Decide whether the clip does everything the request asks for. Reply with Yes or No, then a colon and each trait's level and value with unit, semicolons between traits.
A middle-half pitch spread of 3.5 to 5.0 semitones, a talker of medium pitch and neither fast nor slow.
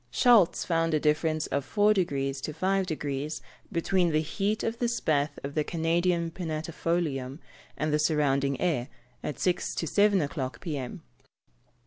Yes: average, 3.8 semitones; medium, 160 Hz; average, 150 wpm